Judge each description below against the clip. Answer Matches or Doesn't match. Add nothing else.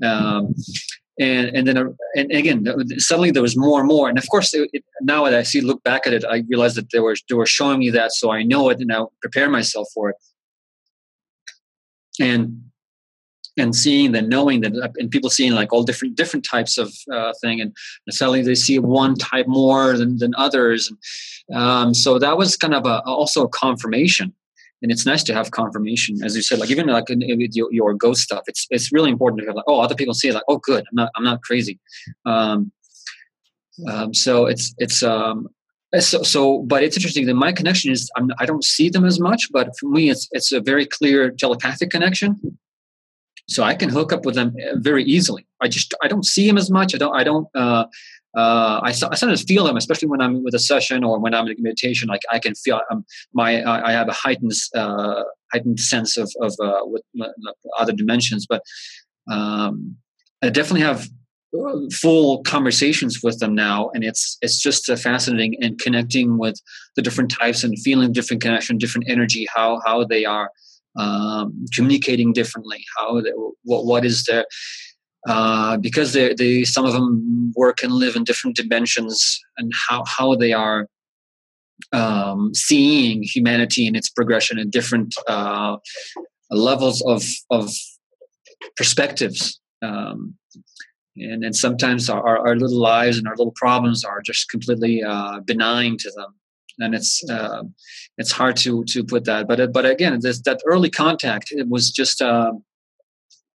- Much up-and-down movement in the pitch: Doesn't match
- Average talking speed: Matches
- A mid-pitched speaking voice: Doesn't match